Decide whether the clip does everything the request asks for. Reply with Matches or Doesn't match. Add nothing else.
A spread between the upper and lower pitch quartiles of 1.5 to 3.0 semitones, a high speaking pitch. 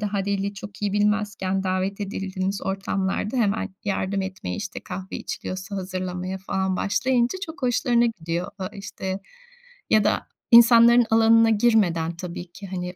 Matches